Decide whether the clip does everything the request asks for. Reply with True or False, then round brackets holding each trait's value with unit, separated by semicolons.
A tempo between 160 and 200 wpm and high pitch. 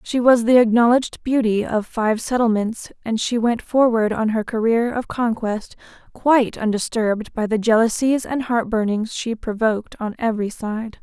True (165 wpm; 225 Hz)